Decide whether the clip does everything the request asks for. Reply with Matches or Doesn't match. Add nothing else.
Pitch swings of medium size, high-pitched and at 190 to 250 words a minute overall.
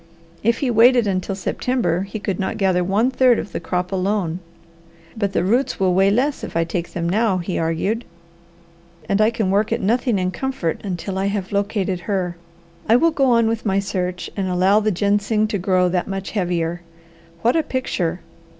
Matches